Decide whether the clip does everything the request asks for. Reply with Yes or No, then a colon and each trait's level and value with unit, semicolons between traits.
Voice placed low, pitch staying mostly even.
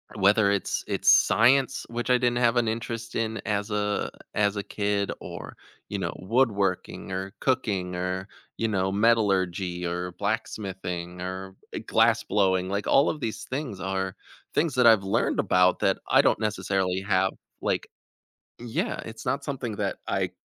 No: low, 100 Hz; average, 3.3 semitones